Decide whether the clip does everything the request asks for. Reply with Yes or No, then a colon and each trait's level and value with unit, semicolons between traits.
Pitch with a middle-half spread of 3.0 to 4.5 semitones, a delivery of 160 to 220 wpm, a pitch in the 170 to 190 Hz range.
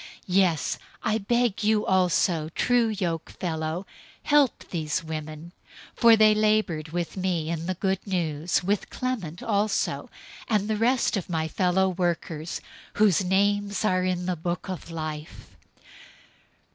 No: average, 4.0 semitones; slow, 135 wpm; medium, 185 Hz